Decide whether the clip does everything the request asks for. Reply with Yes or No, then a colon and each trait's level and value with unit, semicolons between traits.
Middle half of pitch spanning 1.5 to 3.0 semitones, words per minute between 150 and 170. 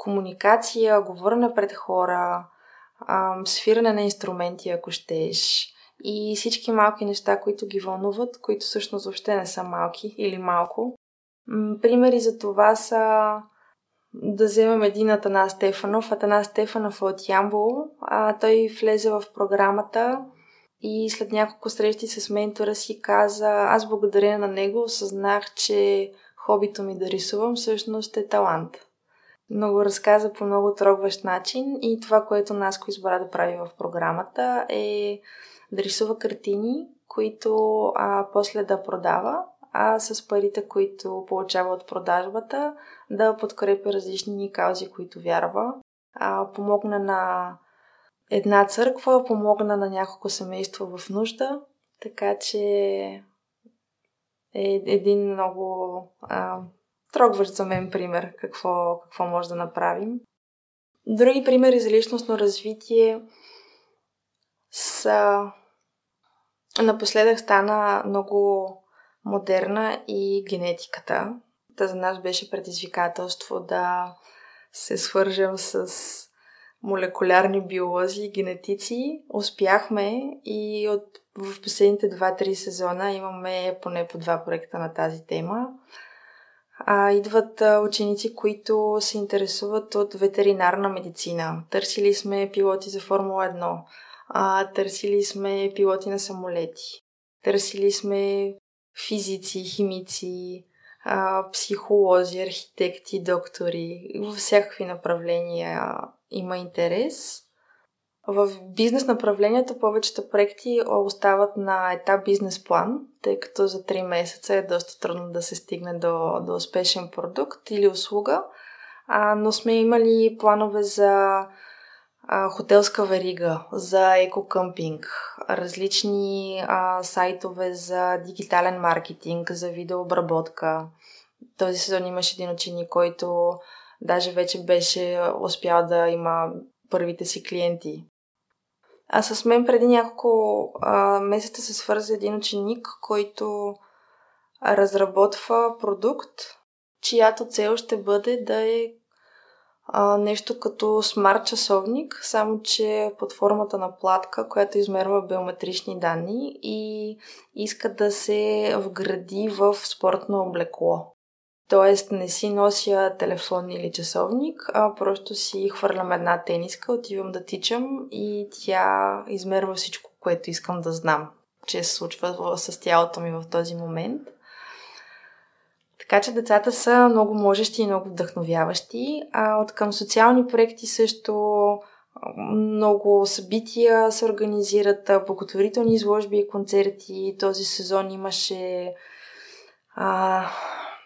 No: average, 2.7 semitones; slow, 115 wpm